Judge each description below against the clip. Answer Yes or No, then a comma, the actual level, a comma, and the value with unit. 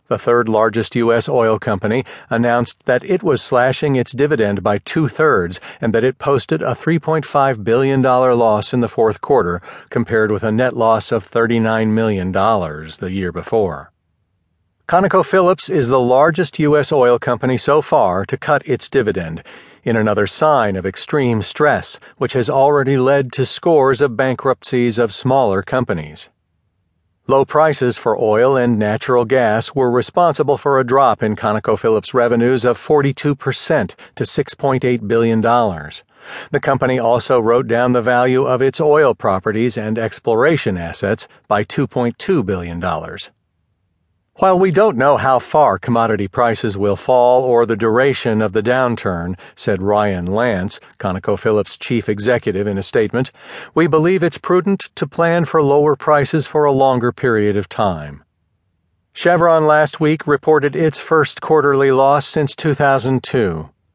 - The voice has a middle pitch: No, low, 125 Hz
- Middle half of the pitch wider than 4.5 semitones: Yes, average, 4.9 semitones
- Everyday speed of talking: Yes, average, 145 wpm